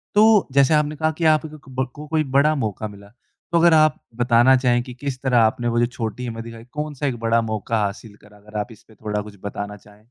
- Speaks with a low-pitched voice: Yes, low, 120 Hz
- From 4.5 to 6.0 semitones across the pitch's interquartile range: Yes, wide, 5.6 semitones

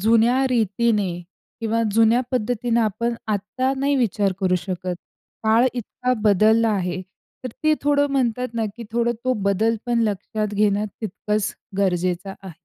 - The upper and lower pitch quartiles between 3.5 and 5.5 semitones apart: No, average, 3.0 semitones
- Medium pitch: No, high, 220 Hz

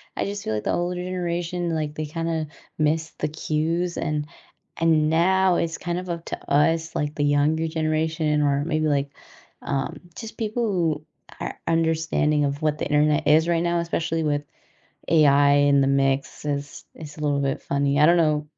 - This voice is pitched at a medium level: Yes, medium, 155 Hz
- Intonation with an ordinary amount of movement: No, narrow, 2.3 semitones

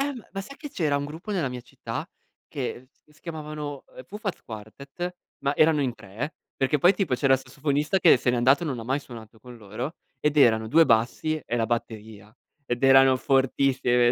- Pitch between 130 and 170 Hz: Yes, low, 135 Hz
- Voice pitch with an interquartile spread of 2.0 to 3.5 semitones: No, average, 4.2 semitones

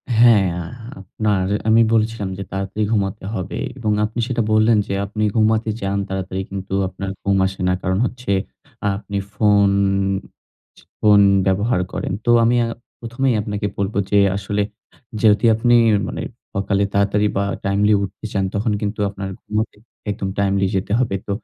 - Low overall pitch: Yes, low, 100 Hz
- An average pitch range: No, narrow, 2.0 semitones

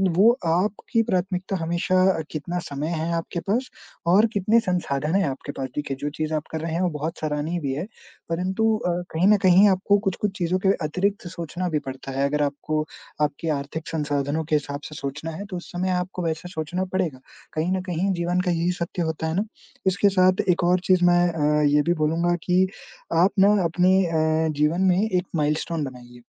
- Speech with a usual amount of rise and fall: Yes, average, 3.2 semitones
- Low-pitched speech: No, medium, 170 Hz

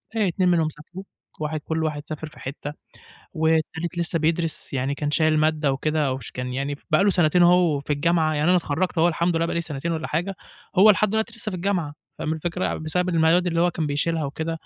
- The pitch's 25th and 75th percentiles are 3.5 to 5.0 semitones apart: No, narrow, 2.5 semitones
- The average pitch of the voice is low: No, medium, 160 Hz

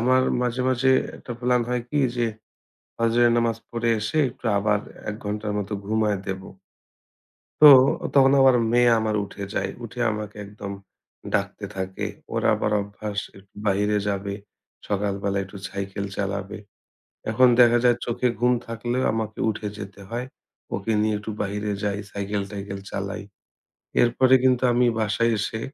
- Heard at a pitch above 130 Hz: No, low, 105 Hz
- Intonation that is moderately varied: Yes, average, 3.1 semitones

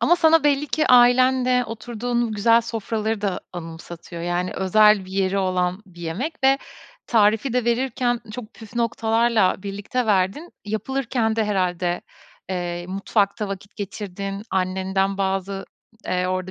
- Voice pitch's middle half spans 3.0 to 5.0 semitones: Yes, average, 4.2 semitones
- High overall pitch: Yes, high, 210 Hz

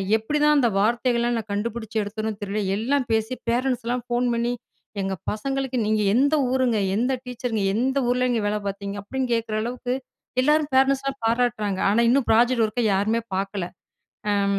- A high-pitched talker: Yes, high, 235 Hz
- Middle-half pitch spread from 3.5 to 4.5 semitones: No, average, 3.0 semitones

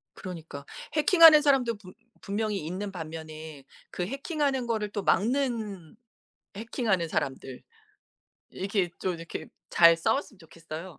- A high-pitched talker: Yes, high, 195 Hz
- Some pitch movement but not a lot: No, wide, 6.1 semitones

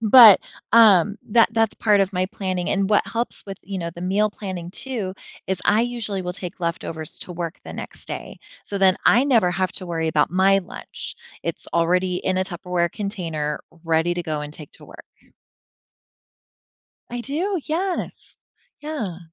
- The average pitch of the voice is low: No, high, 190 Hz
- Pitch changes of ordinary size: Yes, average, 3.7 semitones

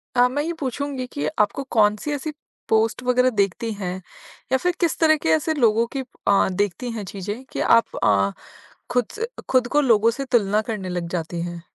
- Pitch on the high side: Yes, high, 230 Hz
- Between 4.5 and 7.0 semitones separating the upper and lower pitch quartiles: Yes, average, 4.8 semitones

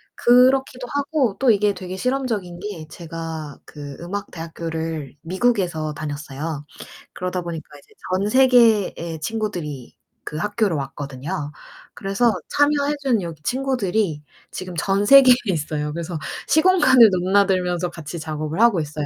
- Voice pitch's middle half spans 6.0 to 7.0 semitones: Yes, wide, 6.5 semitones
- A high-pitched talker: No, medium, 180 Hz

